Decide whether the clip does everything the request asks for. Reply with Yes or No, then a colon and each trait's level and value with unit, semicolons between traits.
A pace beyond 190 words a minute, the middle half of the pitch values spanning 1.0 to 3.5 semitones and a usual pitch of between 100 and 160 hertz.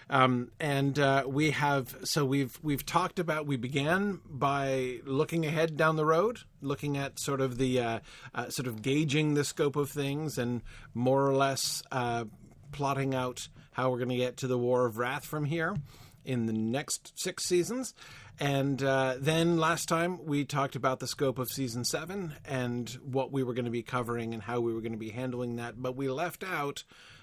Yes: average, 200 wpm; average, 3.0 semitones; low, 135 Hz